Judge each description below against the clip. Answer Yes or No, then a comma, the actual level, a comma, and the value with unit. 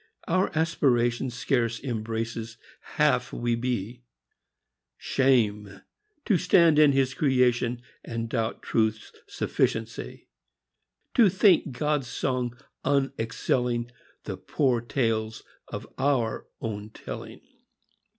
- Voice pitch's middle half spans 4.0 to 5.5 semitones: No, average, 3.1 semitones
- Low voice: Yes, low, 120 Hz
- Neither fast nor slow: No, slow, 95 wpm